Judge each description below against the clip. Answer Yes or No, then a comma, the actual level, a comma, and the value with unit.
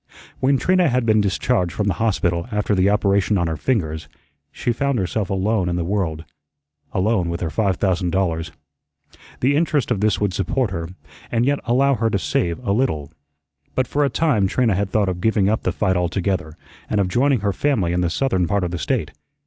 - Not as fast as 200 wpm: No, fast, 205 wpm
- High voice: No, low, 100 Hz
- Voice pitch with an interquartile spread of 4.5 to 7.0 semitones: Yes, average, 5.0 semitones